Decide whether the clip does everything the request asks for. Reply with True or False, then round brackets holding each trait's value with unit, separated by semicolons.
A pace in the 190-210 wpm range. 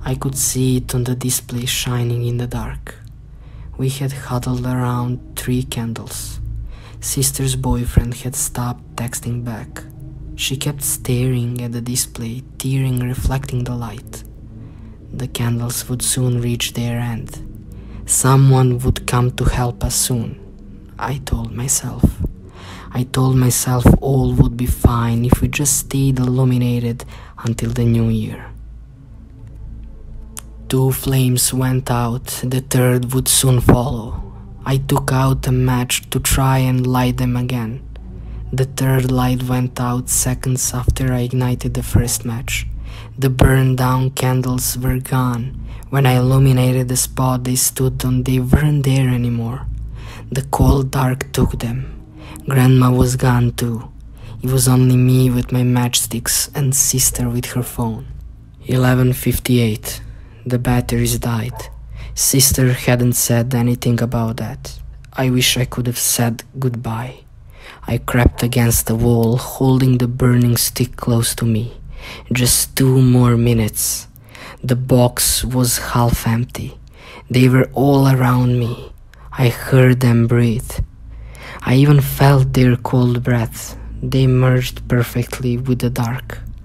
False (135 wpm)